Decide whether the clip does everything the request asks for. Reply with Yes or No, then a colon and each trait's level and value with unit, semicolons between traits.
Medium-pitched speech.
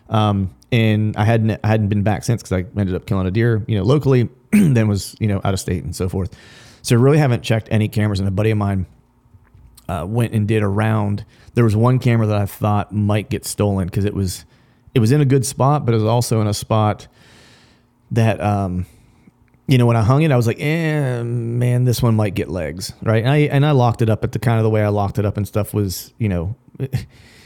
No: low, 110 Hz